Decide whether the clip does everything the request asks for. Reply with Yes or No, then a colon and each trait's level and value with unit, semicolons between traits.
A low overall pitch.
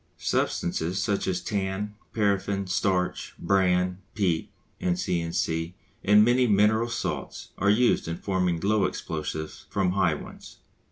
Yes: very low, 95 Hz